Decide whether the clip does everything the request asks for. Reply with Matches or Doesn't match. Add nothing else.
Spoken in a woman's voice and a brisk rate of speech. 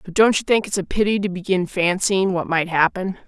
Matches